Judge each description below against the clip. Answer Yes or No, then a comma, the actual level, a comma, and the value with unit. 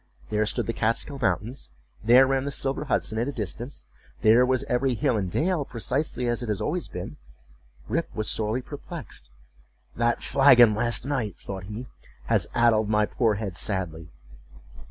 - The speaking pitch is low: Yes, low, 115 Hz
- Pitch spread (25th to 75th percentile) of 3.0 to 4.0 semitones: No, average, 4.4 semitones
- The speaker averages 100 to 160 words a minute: Yes, average, 150 wpm